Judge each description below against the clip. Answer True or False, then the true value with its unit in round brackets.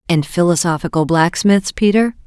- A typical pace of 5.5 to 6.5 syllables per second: False (5.1 syllables/s)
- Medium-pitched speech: True (180 Hz)